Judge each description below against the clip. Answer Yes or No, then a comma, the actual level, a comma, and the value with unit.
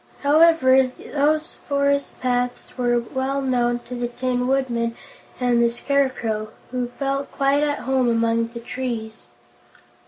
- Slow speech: Yes, slow, 130 wpm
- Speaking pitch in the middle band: No, very high, 255 Hz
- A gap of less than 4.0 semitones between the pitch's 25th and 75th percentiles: Yes, narrow, 2.5 semitones